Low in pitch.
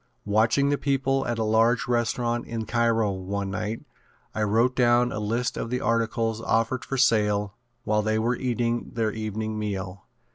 Yes: low, 115 Hz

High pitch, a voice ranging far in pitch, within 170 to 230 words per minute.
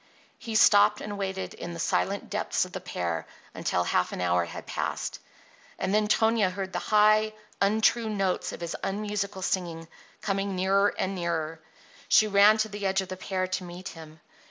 No: high, 195 Hz; average, 3.3 semitones; average, 185 wpm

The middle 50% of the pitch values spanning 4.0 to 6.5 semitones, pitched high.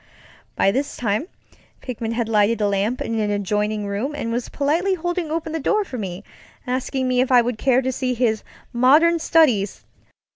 Yes: average, 5.2 semitones; very high, 250 Hz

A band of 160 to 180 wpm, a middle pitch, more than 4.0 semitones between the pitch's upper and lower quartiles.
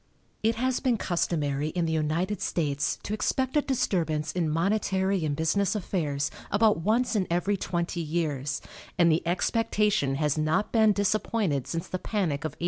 Yes: average, 165 wpm; medium, 175 Hz; average, 5.3 semitones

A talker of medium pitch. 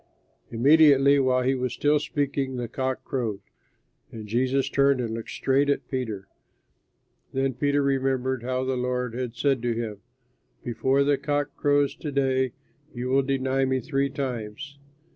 No: low, 130 Hz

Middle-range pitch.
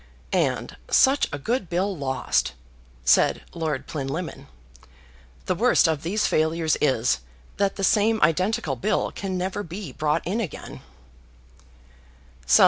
Yes: medium, 170 Hz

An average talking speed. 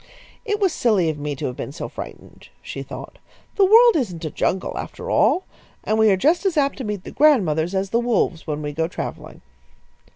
No: fast, 215 wpm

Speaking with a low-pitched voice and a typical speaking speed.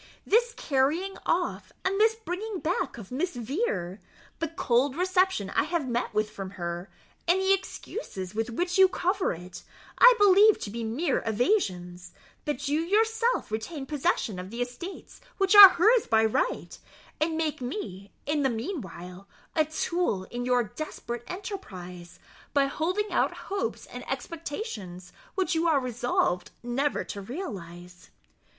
No: very high, 280 Hz; average, 150 wpm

